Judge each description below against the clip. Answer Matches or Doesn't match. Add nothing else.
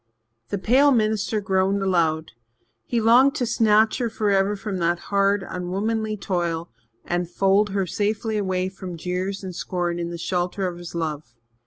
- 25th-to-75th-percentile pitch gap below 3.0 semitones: Doesn't match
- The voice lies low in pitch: Doesn't match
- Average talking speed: Matches